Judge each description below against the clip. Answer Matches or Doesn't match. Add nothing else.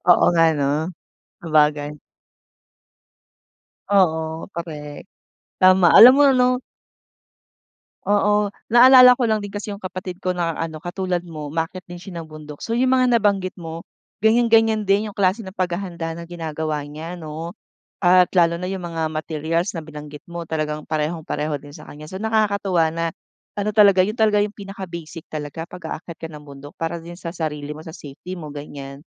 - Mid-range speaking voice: Matches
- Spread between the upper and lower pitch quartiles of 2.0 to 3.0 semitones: Doesn't match